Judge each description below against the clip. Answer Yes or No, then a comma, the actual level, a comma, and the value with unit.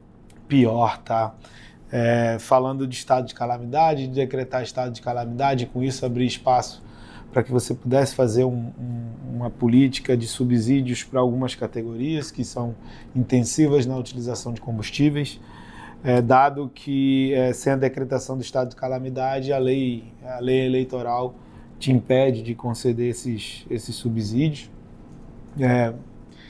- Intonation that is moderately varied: No, narrow, 1.8 semitones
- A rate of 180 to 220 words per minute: No, average, 140 wpm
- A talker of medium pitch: No, low, 125 Hz